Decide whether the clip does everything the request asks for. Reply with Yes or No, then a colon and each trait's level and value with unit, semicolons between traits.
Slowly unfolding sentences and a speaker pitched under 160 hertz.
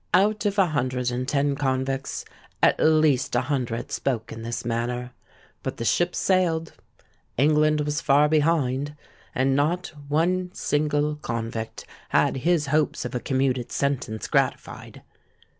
Yes: slow, 130 wpm; medium, 140 Hz